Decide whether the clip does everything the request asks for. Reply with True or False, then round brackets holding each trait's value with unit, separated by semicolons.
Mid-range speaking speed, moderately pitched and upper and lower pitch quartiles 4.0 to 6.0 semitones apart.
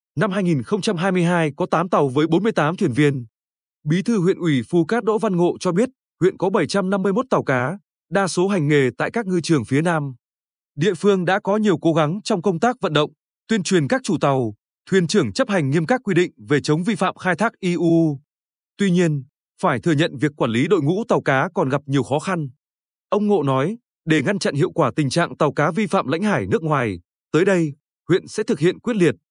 True (225 wpm; 175 Hz; 5.1 semitones)